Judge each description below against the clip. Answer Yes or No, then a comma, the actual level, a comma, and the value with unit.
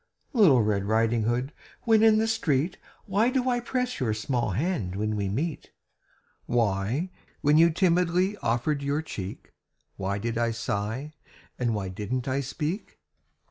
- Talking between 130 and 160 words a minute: Yes, average, 150 wpm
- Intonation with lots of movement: Yes, wide, 8.4 semitones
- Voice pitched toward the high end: No, low, 130 Hz